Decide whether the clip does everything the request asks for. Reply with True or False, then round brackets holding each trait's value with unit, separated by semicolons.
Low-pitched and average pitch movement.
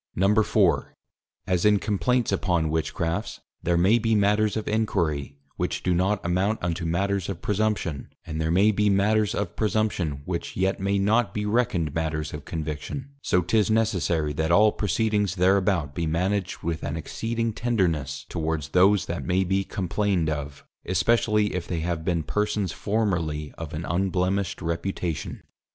True (95 Hz; 4.2 semitones)